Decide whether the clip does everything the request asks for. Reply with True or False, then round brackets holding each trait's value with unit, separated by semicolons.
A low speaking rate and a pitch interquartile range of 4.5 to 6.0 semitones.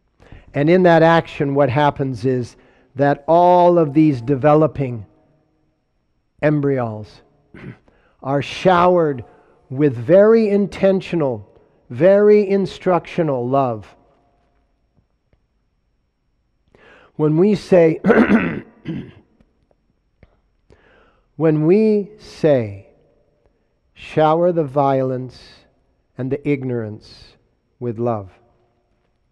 True (70 wpm; 5.4 semitones)